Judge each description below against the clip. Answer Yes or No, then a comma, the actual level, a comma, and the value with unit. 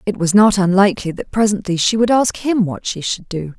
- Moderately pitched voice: No, high, 195 Hz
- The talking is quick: Yes, fast, 235 wpm